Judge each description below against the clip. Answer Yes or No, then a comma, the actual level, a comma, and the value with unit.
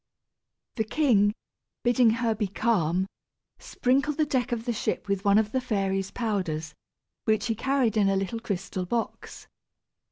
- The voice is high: Yes, high, 220 Hz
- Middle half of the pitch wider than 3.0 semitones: Yes, average, 3.6 semitones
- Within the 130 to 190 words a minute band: Yes, average, 155 wpm